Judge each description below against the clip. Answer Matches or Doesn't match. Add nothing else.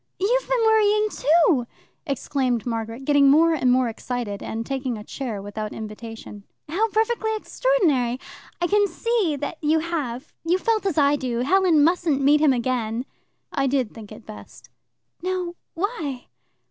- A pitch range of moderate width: Doesn't match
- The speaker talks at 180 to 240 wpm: Doesn't match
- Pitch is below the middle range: Doesn't match